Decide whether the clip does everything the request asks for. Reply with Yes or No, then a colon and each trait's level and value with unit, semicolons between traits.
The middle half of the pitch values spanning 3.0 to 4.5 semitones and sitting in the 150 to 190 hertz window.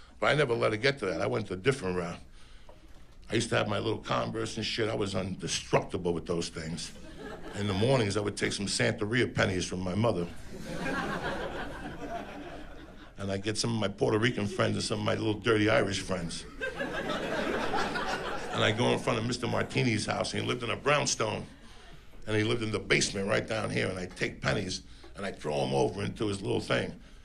No: average, 3.4 semitones; low, 105 Hz